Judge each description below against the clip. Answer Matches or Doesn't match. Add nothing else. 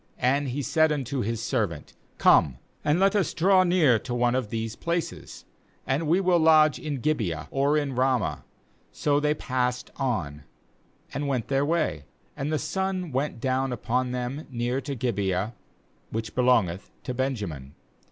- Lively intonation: Doesn't match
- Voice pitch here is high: Doesn't match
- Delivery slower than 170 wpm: Matches